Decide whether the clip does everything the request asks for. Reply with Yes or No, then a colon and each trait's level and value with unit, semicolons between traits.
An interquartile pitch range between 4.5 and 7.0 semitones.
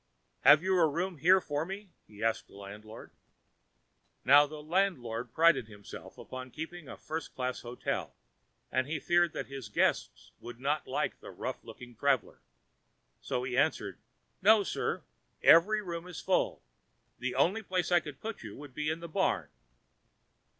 Yes: wide, 5.6 semitones